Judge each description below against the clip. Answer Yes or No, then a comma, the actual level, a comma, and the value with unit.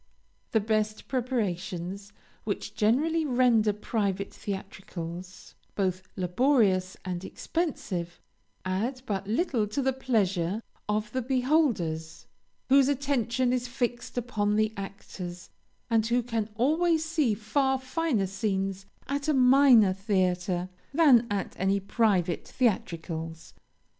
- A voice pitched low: No, high, 215 Hz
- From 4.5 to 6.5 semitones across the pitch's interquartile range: Yes, average, 5.1 semitones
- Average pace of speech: No, slow, 115 wpm